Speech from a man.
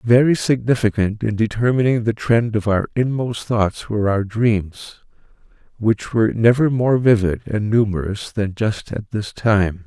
Yes: male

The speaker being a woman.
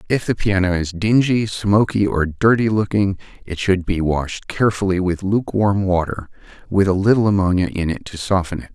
No: male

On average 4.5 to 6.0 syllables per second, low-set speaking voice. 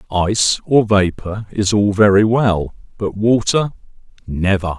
No: 4.0 syllables/s; low, 100 Hz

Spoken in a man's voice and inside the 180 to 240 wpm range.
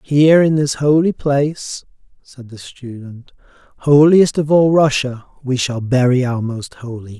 No: male; average, 150 wpm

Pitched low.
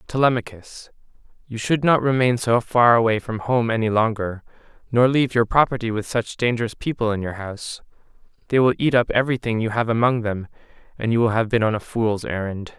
Yes: low, 115 Hz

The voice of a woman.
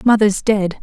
Yes: female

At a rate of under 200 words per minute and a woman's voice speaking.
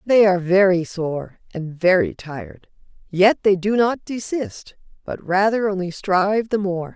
Yes: average, 155 wpm; female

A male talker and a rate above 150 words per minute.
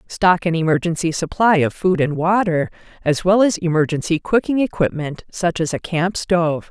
No: female; average, 170 wpm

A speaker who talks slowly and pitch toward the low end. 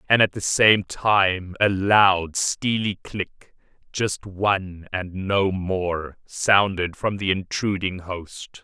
Yes: slow, 130 wpm; very low, 95 Hz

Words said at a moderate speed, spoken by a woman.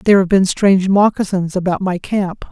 Yes: average, 190 wpm; female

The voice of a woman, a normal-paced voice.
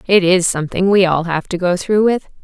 No: female; fast, 245 wpm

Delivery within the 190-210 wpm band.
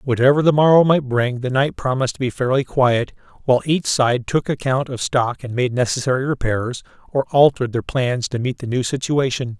Yes: average, 200 wpm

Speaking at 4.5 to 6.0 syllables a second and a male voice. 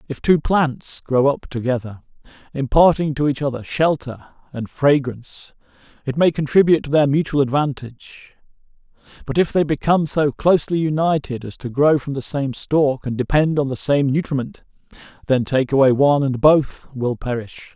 Yes: 5.0 syllables/s; male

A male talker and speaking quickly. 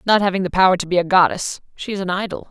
No: female; fast, 285 wpm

